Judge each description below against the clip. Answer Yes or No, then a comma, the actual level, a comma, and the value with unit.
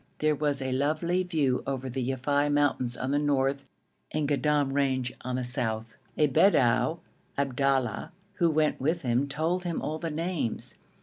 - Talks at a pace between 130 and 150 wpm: No, average, 165 wpm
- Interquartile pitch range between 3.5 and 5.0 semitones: No, average, 2.9 semitones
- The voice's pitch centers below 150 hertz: Yes, medium, 140 Hz